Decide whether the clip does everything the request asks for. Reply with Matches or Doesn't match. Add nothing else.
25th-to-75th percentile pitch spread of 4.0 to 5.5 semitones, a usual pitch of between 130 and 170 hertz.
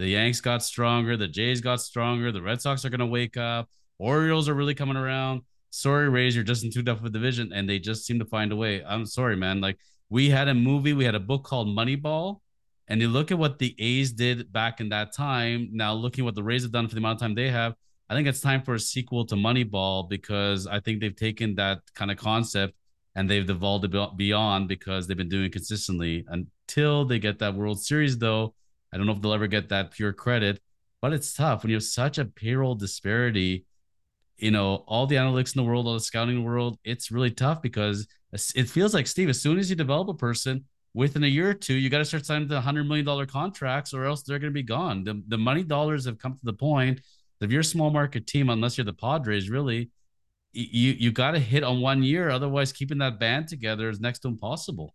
Doesn't match